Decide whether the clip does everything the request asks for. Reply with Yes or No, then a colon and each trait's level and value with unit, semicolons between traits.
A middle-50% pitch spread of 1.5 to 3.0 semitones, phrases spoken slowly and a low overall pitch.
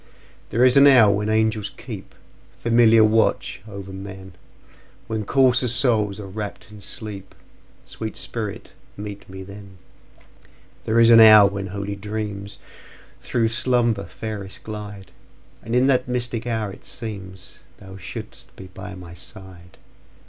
Yes: narrow, 2.6 semitones; slow, 120 wpm; low, 105 Hz